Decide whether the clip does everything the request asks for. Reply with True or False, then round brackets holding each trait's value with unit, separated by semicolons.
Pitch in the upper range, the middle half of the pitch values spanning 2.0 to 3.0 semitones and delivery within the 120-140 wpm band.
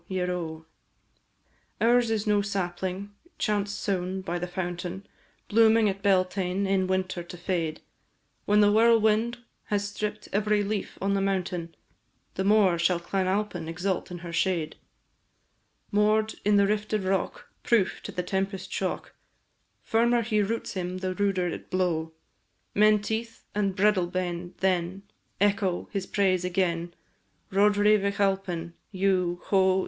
True (195 Hz; 2.5 semitones; 135 wpm)